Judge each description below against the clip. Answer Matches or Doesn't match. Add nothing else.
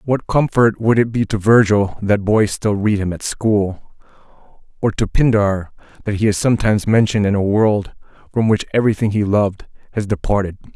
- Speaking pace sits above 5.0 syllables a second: Matches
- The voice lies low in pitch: Matches